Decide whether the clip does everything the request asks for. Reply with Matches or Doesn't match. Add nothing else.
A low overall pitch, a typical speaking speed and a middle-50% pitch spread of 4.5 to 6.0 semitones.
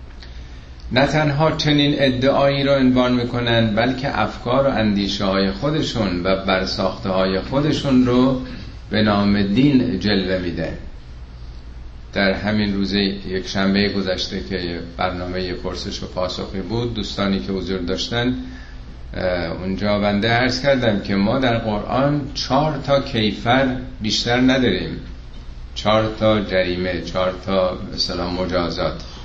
Matches